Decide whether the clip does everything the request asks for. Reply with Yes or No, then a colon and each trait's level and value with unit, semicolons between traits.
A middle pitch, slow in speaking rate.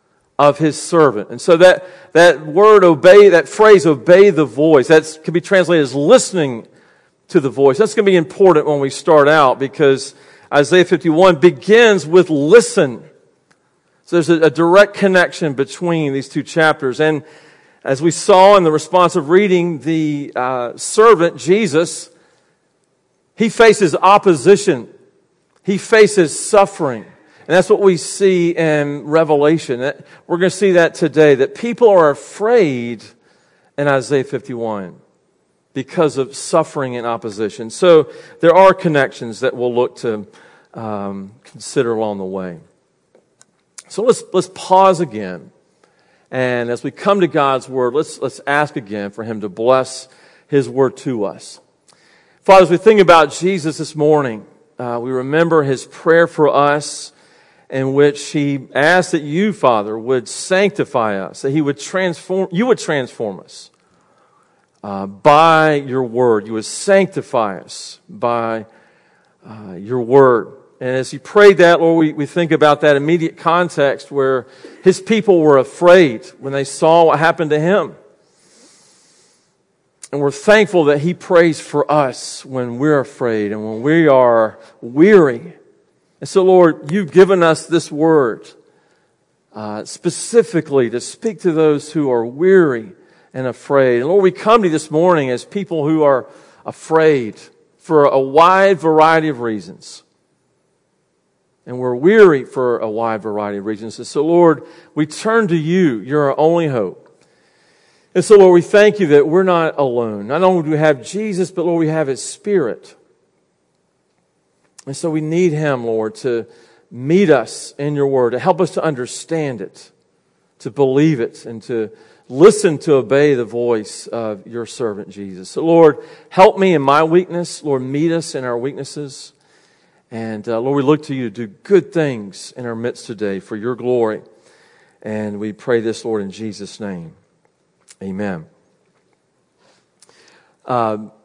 No: medium, 150 Hz; average, 155 wpm